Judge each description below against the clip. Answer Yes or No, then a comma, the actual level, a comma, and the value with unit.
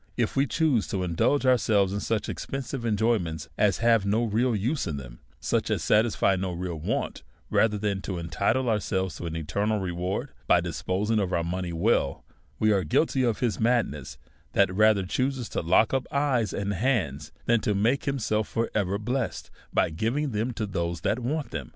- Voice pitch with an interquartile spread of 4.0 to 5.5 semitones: Yes, average, 4.5 semitones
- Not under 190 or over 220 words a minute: Yes, average, 195 wpm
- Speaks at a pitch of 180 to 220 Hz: No, low, 105 Hz